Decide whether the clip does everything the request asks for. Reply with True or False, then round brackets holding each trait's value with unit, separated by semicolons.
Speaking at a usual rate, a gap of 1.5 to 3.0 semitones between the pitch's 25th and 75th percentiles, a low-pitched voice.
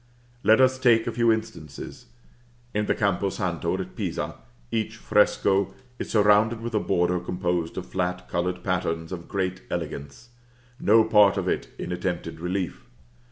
False (155 wpm; 3.6 semitones; 95 Hz)